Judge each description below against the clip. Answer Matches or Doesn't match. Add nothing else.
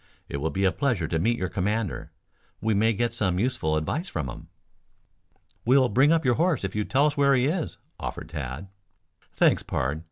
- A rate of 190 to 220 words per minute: Matches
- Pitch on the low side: Matches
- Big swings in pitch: Matches